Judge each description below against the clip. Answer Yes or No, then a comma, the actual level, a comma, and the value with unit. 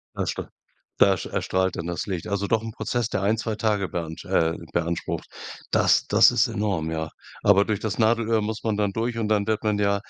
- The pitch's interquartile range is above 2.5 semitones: Yes, average, 2.9 semitones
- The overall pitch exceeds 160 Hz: No, low, 105 Hz